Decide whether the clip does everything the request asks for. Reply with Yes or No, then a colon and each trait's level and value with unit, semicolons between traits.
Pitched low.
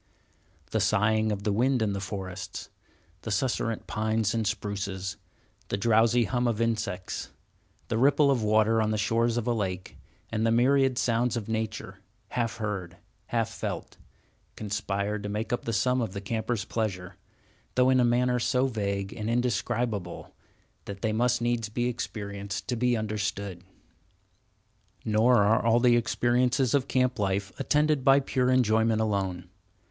Yes: low, 110 Hz